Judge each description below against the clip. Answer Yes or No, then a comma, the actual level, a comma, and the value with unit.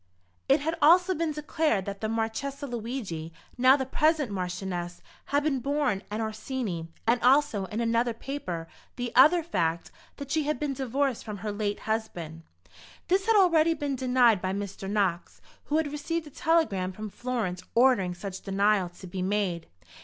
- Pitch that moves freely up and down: Yes, wide, 6.9 semitones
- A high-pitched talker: Yes, high, 235 Hz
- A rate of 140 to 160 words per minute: No, average, 170 wpm